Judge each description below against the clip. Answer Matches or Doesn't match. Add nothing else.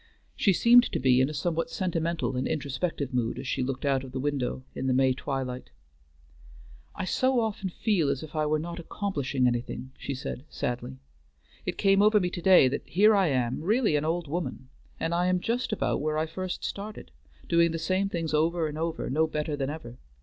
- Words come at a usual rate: Doesn't match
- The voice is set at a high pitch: Doesn't match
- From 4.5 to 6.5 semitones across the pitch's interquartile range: Matches